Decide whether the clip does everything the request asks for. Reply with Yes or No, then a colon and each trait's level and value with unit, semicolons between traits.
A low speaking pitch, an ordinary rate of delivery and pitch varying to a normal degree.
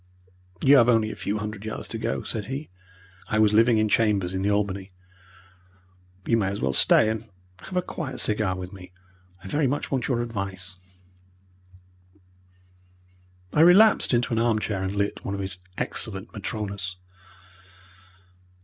Yes: low, 105 Hz; average, 160 wpm; average, 3.2 semitones